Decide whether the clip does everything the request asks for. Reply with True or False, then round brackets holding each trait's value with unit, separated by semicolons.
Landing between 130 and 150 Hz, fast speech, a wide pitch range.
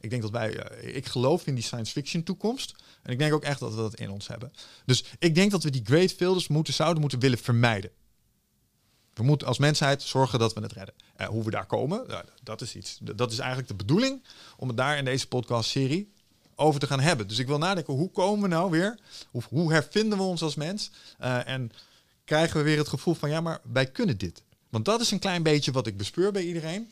True (140 Hz; 245 wpm; 5.9 semitones)